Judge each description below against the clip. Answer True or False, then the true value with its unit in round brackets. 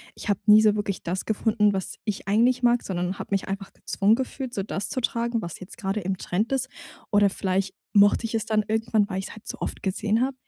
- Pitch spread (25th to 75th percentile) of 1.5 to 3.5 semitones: True (2.7 semitones)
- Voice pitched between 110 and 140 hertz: False (210 Hz)